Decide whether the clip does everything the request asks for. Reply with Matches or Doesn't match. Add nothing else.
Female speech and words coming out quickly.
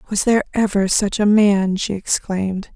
Doesn't match